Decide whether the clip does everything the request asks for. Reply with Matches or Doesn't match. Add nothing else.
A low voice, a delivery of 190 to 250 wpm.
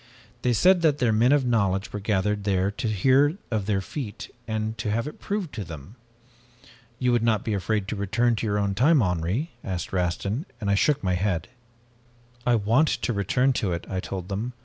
Matches